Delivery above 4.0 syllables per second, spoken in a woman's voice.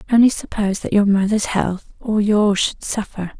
Yes: 4.9 syllables/s; female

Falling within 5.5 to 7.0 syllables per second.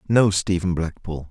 No: 4.4 syllables/s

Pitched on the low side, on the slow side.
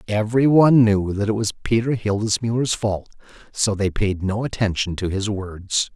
No: low, 105 Hz; average, 170 wpm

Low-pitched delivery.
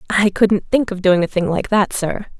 No: high, 195 Hz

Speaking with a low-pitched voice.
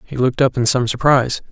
Yes: low, 130 Hz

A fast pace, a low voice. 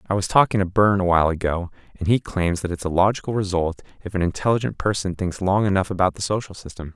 Yes: fast, 225 wpm; very low, 95 Hz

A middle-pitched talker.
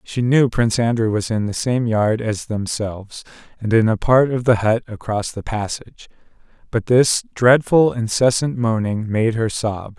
No: low, 115 Hz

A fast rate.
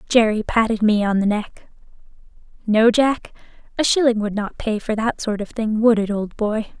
No: average, 195 wpm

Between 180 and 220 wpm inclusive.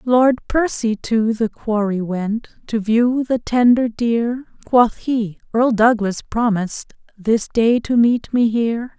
No: average, 145 wpm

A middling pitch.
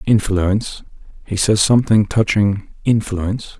No: low, 105 Hz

